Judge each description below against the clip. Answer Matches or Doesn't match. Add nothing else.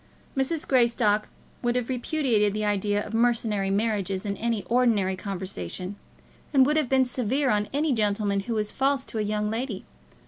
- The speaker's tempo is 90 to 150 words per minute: Doesn't match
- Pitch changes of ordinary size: Matches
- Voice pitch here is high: Matches